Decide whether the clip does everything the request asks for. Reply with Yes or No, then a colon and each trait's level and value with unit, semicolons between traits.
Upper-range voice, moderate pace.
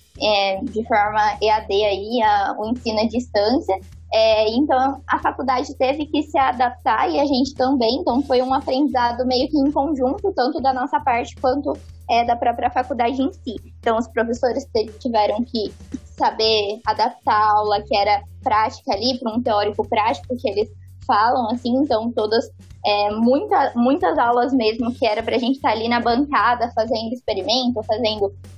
Yes: high, 240 Hz; average, 170 wpm